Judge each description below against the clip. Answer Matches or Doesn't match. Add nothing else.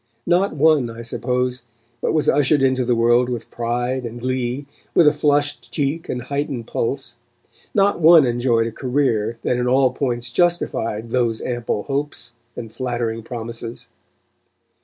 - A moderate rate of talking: Matches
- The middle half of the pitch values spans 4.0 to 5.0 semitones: Doesn't match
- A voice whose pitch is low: Matches